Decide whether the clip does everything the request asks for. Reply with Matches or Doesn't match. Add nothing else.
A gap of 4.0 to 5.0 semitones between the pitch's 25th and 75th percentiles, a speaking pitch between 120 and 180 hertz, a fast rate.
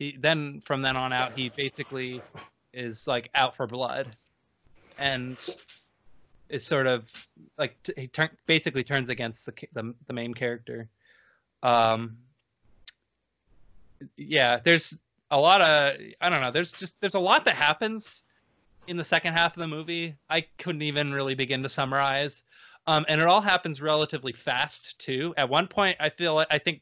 Doesn't match